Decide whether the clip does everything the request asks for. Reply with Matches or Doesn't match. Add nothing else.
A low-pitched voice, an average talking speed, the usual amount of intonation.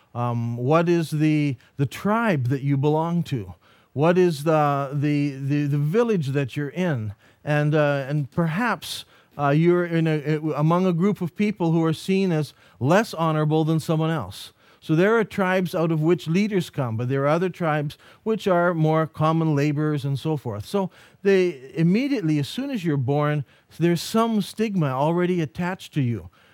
Doesn't match